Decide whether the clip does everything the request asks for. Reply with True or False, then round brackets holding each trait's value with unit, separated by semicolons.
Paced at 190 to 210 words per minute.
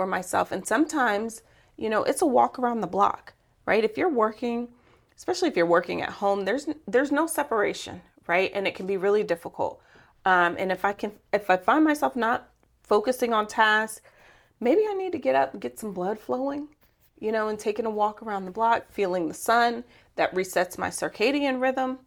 True (200 wpm)